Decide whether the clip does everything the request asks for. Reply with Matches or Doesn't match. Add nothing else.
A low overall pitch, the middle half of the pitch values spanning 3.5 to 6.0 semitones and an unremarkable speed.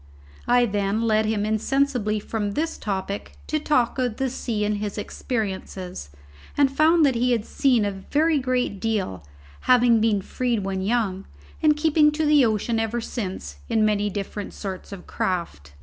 Doesn't match